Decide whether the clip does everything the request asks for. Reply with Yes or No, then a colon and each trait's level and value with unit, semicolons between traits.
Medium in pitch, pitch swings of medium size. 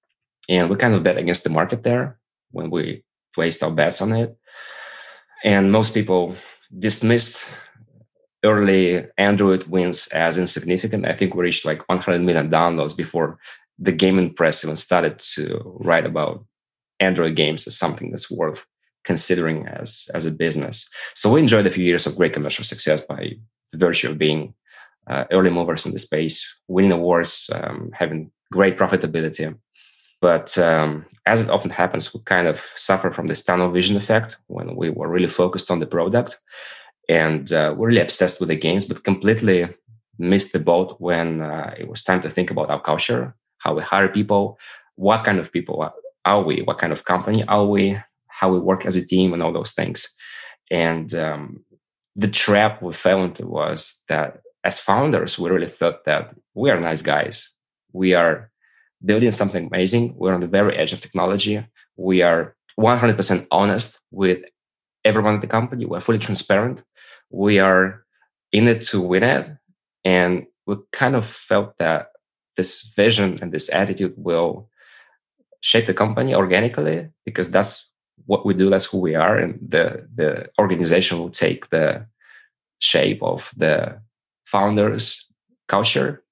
No: very low, 95 Hz; average, 3.7 semitones